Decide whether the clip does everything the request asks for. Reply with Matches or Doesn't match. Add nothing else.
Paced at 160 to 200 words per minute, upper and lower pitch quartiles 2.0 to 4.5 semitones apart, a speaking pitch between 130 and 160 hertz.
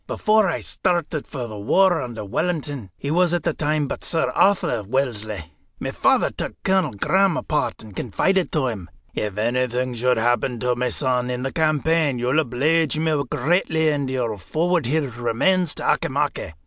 Doesn't match